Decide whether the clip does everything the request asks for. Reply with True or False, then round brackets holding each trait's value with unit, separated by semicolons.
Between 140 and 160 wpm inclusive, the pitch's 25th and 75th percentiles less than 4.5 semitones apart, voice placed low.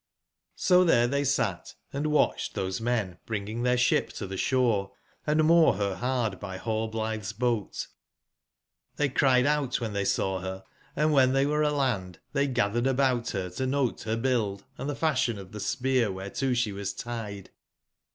False (155 wpm; 5.0 semitones; 120 Hz)